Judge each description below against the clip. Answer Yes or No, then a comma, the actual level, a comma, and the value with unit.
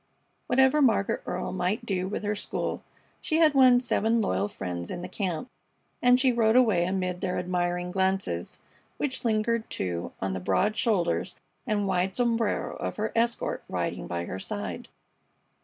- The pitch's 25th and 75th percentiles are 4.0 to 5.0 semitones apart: Yes, average, 4.7 semitones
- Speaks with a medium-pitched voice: No, high, 200 Hz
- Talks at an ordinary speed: Yes, average, 160 wpm